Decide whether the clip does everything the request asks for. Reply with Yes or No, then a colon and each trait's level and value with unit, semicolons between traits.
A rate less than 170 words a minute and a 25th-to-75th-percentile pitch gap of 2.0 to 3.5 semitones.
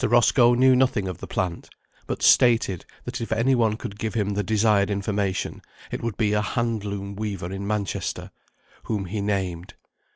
No: average, 175 wpm; narrow, 2.5 semitones